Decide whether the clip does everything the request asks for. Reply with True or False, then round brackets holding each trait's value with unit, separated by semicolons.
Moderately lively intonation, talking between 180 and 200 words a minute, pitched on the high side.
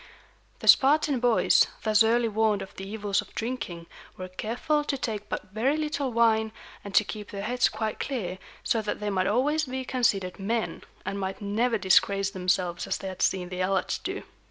True (4.2 semitones; 190 wpm; 215 Hz)